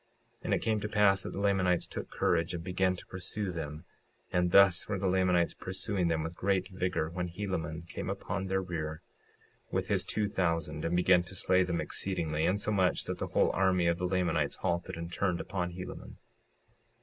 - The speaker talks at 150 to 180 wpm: No, average, 195 wpm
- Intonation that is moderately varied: No, narrow, 2.1 semitones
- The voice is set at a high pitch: No, very low, 90 Hz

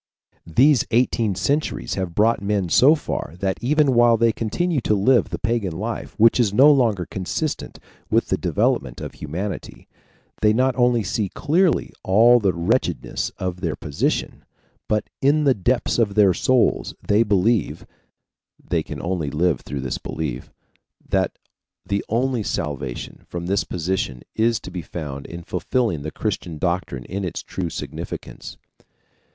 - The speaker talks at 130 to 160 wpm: Yes, average, 155 wpm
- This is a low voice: Yes, low, 105 Hz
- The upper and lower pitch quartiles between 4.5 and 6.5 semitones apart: Yes, wide, 5.5 semitones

